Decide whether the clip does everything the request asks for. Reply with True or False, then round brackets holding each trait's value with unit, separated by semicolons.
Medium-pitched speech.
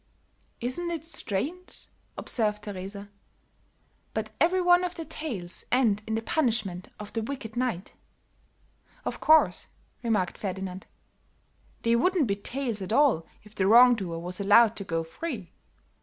False (220 Hz)